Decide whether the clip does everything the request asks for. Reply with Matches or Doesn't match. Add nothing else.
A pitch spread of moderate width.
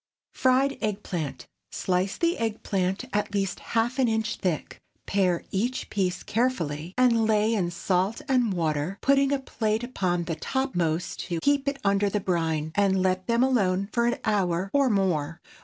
Matches